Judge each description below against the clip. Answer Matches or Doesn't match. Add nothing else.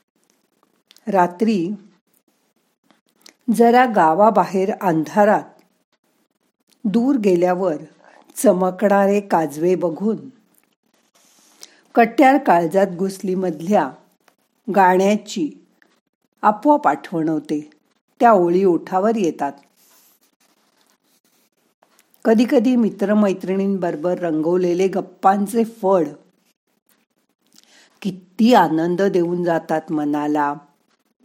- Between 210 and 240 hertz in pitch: Doesn't match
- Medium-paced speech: Doesn't match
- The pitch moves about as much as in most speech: Matches